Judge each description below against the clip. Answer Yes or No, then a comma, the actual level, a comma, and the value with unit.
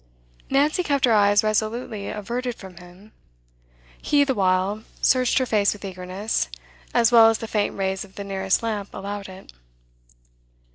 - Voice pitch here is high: Yes, high, 210 Hz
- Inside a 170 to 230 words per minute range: No, average, 155 wpm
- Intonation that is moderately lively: Yes, average, 3.3 semitones